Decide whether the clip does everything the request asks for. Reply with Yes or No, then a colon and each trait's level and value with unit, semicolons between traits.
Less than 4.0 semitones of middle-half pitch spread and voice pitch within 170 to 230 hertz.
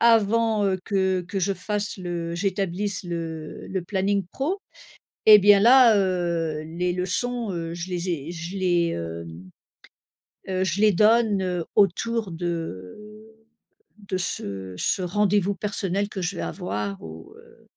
Yes: average, 3.3 semitones; medium, 185 Hz